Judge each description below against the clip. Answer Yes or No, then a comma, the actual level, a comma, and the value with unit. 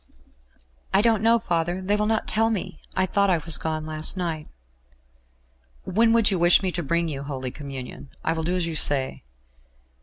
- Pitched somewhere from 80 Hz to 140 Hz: No, medium, 175 Hz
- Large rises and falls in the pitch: No, average, 4.3 semitones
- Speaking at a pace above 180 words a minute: Yes, average, 190 wpm